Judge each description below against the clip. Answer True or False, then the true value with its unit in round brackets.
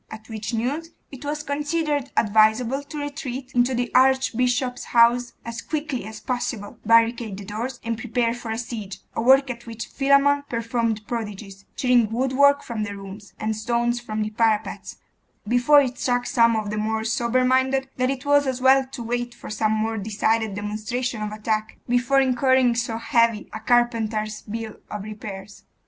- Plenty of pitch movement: False (2.9 semitones)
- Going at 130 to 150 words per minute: False (170 wpm)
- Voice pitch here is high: True (235 Hz)